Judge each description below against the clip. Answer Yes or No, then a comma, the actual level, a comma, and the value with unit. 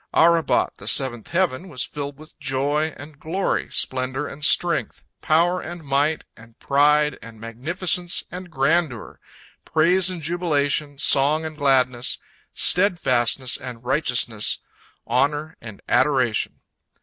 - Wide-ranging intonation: No, average, 4.1 semitones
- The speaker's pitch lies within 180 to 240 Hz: No, medium, 145 Hz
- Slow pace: Yes, slow, 120 wpm